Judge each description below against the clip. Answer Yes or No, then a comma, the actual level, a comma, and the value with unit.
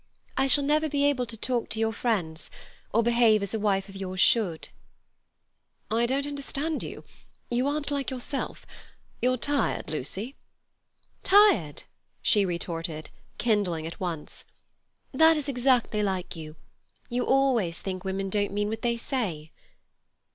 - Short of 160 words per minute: Yes, average, 145 wpm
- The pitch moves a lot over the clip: Yes, wide, 6.1 semitones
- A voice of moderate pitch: No, high, 225 Hz